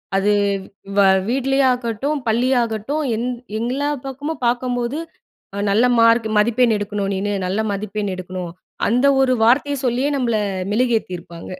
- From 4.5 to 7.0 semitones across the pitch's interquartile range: No, average, 3.7 semitones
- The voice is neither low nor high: No, high, 235 Hz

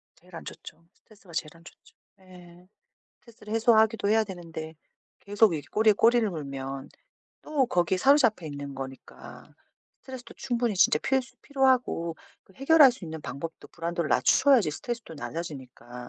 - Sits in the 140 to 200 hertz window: Yes, medium, 185 Hz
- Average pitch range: No, wide, 6.7 semitones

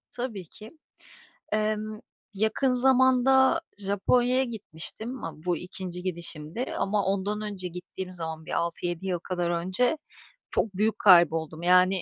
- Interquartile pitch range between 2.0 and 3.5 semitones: No, average, 4.2 semitones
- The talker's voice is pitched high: Yes, high, 195 Hz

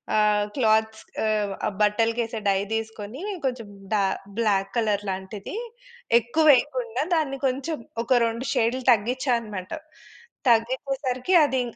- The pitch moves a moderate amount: Yes, average, 3.5 semitones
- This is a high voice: Yes, high, 230 Hz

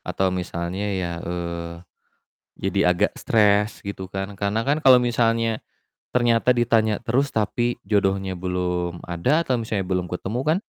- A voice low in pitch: Yes, low, 100 Hz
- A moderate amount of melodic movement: Yes, average, 4.6 semitones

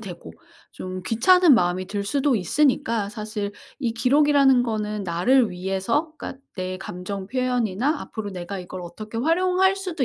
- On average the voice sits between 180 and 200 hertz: No, high, 220 Hz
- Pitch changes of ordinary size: No, wide, 6.4 semitones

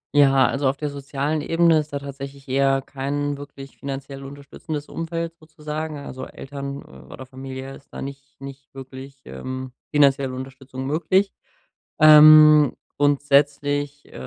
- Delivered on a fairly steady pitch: Yes, narrow, 1.6 semitones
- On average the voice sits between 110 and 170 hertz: Yes, medium, 140 Hz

